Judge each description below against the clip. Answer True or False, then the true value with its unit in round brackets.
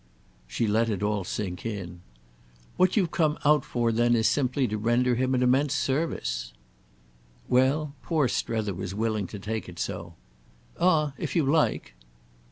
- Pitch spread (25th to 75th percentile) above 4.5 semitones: True (5.5 semitones)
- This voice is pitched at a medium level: False (120 Hz)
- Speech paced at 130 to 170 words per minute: True (160 wpm)